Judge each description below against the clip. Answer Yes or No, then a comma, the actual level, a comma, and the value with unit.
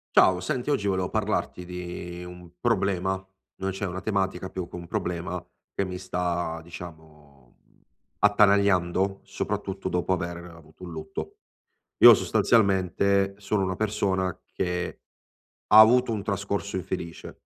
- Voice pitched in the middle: No, very low, 95 Hz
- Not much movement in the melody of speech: Yes, narrow, 2.3 semitones